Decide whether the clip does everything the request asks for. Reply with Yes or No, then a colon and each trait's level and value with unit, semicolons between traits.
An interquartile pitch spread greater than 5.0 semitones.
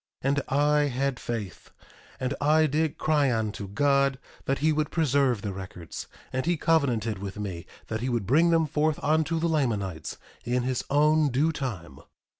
Yes: wide, 5.4 semitones